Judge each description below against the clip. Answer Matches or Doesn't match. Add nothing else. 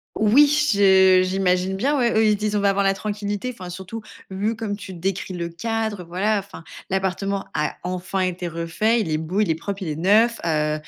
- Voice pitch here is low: Doesn't match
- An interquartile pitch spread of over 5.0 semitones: Doesn't match